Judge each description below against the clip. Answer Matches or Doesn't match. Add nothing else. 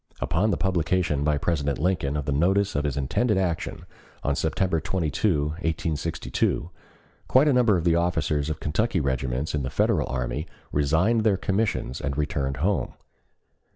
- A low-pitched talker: Matches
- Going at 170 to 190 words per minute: Doesn't match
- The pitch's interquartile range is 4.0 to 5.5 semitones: Matches